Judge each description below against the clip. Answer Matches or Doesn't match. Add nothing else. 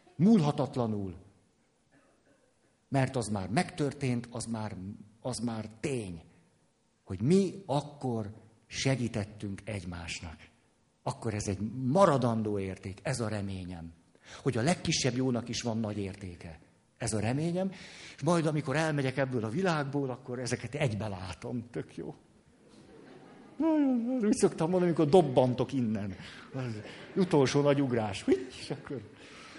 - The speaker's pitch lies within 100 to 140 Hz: Matches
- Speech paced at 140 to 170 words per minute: Doesn't match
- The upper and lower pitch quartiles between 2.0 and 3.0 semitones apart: Doesn't match